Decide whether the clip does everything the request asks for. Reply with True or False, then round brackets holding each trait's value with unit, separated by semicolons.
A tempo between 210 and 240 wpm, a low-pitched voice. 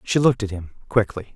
True (220 wpm; 105 Hz)